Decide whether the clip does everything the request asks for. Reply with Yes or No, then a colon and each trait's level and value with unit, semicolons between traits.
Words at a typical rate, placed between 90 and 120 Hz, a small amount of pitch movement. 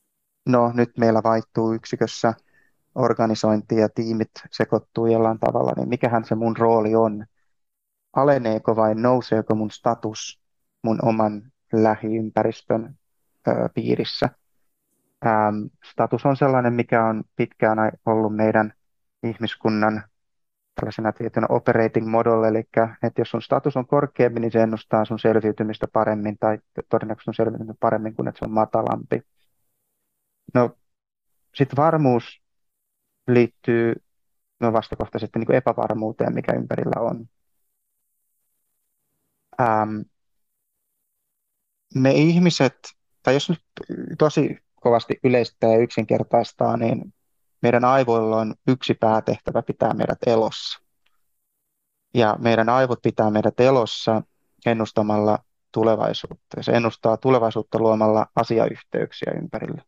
Yes: average, 110 wpm; low, 115 Hz; narrow, 1.6 semitones